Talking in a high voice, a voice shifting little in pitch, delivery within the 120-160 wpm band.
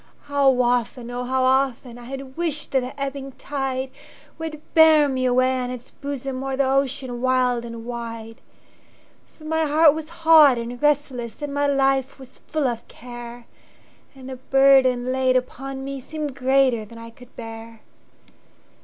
Yes: very high, 260 Hz; narrow, 2.1 semitones; average, 140 wpm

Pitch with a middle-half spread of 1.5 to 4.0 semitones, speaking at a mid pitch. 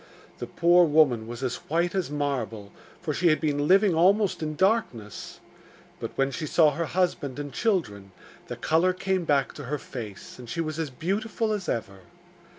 No: average, 5.3 semitones; medium, 155 Hz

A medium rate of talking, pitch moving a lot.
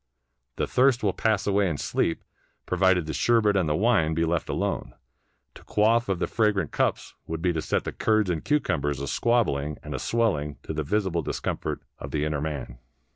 No: fast, 210 wpm; wide, 5.9 semitones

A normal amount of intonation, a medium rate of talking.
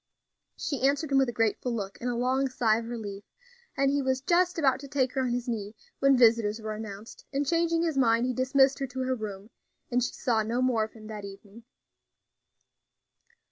No: average, 3.6 semitones; fast, 210 wpm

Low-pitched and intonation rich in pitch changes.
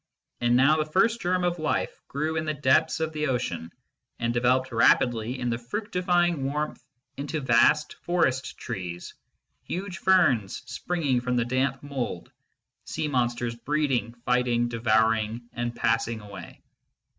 No: low, 130 Hz; average, 4.6 semitones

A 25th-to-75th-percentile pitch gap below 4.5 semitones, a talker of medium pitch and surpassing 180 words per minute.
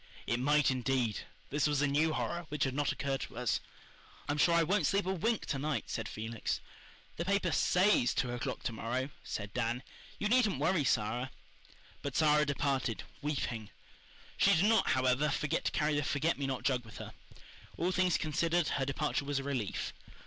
Yes: average, 3.7 semitones; medium, 145 Hz; average, 190 wpm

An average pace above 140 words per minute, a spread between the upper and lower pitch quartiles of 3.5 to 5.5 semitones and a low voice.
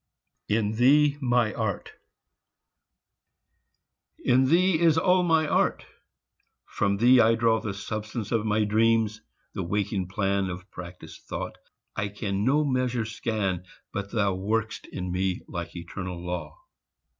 No: slow, 135 wpm; average, 4.1 semitones; low, 110 Hz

